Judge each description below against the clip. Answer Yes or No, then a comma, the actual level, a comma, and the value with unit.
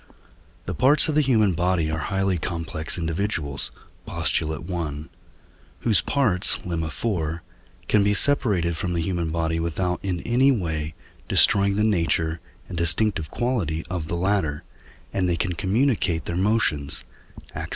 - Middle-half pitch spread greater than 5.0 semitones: No, average, 4.1 semitones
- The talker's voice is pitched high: No, very low, 90 Hz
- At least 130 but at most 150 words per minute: Yes, average, 145 wpm